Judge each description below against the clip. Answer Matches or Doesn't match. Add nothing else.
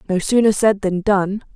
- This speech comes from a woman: Matches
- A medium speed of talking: Matches